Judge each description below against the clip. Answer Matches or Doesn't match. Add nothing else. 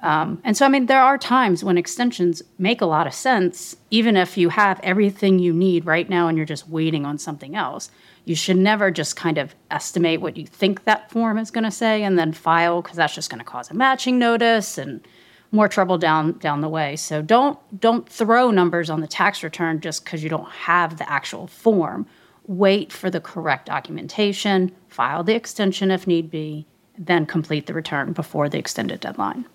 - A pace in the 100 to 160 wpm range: Doesn't match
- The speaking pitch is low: Doesn't match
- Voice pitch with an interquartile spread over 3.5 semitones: Matches